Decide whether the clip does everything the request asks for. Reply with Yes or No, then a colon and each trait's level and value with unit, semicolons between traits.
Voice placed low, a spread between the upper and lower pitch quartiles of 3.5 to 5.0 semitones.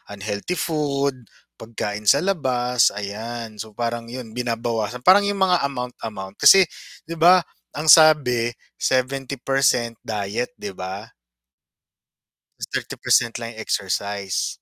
Yes: low, 120 Hz; average, 4.2 semitones